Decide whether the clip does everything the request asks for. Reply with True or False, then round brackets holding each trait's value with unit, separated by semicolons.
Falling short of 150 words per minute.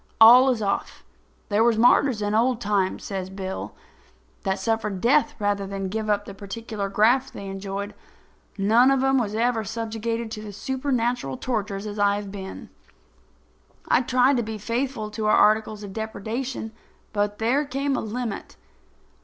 False (165 wpm)